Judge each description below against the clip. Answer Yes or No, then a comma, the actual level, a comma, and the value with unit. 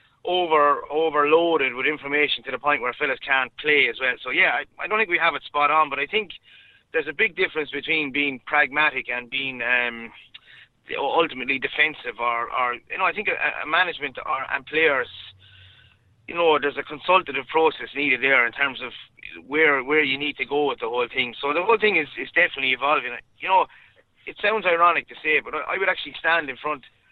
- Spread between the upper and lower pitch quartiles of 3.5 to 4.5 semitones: Yes, average, 4.2 semitones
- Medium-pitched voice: Yes, medium, 145 Hz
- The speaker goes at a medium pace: No, fast, 210 wpm